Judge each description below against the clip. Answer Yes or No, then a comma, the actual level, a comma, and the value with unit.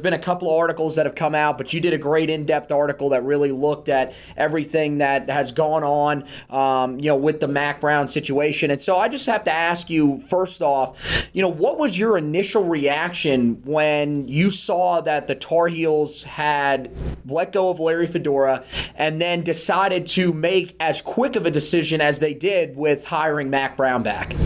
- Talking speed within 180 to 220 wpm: Yes, average, 200 wpm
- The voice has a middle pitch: Yes, medium, 150 Hz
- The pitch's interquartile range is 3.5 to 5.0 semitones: No, average, 3.1 semitones